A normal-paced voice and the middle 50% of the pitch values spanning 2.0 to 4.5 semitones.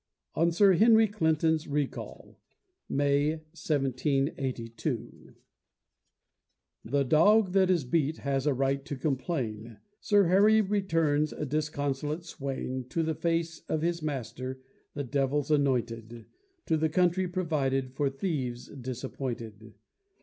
No: slow, 115 wpm; average, 4.0 semitones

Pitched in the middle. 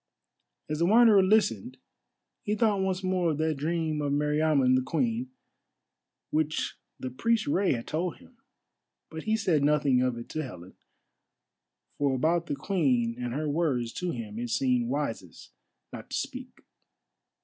Yes: medium, 150 Hz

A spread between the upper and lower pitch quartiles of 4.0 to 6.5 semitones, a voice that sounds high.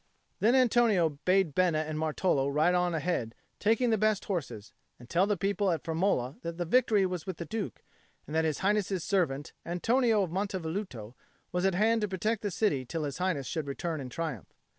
No: average, 4.5 semitones; medium, 180 Hz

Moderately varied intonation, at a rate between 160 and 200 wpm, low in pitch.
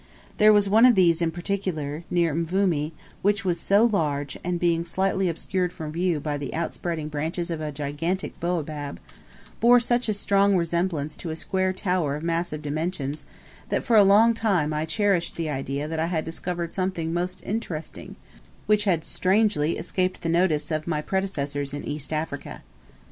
No: average, 3.7 semitones; average, 175 wpm; medium, 170 Hz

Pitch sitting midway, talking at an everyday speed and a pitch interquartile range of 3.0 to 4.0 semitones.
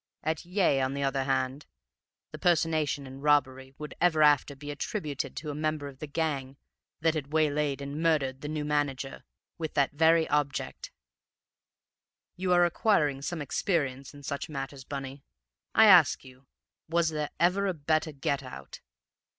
No: medium, 145 Hz; average, 160 wpm; narrow, 2.6 semitones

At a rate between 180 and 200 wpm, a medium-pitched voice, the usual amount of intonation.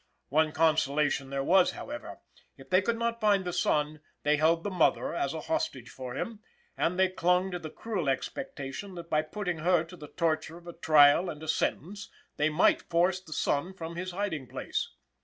Yes: average, 195 wpm; medium, 170 Hz; average, 3.5 semitones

